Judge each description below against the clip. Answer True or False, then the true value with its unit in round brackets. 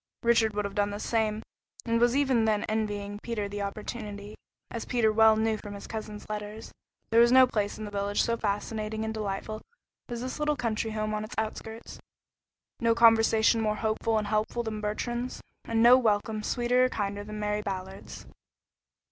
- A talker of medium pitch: False (220 Hz)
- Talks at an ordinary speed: True (180 wpm)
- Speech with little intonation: True (1.8 semitones)